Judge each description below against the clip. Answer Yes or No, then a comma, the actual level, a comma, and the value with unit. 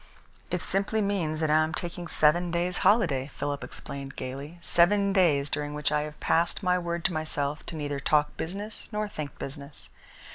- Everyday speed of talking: Yes, average, 180 wpm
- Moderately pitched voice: Yes, medium, 155 Hz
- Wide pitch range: No, average, 3.6 semitones